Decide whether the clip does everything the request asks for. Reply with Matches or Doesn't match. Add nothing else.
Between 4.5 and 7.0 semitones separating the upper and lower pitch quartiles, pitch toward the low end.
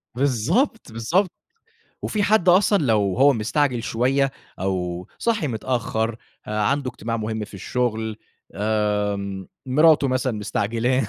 Matches